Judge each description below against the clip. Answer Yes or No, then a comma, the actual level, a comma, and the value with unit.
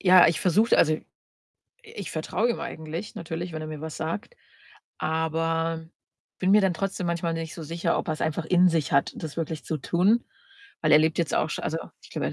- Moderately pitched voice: Yes, medium, 165 Hz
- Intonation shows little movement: Yes, narrow, 2.2 semitones